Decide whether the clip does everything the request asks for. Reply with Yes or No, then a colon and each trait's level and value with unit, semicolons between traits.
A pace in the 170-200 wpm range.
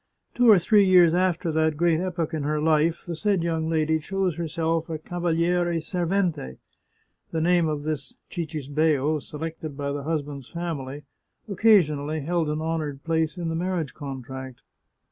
No: average, 160 wpm